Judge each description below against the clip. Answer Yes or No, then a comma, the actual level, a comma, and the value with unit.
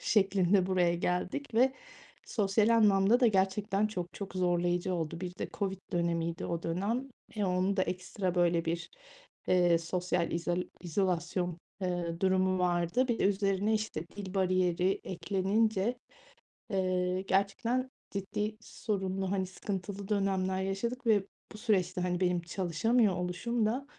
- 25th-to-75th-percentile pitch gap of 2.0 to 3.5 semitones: Yes, narrow, 2.5 semitones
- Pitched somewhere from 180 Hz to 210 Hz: Yes, high, 190 Hz